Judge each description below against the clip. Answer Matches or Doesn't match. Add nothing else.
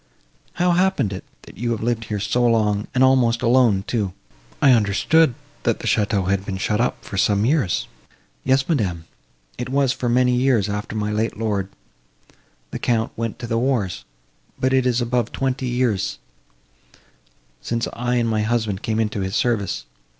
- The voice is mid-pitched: Doesn't match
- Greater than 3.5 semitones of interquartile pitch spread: Doesn't match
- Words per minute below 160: Doesn't match